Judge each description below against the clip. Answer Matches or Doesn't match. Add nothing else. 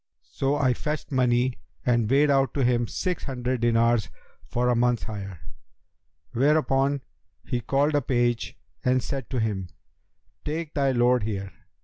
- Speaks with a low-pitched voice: Matches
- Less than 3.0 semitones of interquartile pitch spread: Matches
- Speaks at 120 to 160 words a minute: Matches